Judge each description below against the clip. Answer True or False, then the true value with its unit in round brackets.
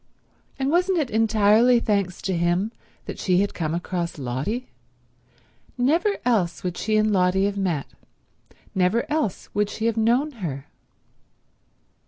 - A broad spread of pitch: False (4.8 semitones)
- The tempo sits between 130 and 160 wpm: True (140 wpm)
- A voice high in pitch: True (205 Hz)